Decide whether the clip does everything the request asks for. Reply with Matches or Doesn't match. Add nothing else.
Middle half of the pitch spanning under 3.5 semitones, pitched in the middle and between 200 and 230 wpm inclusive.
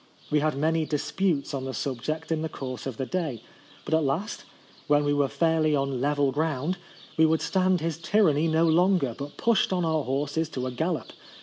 Matches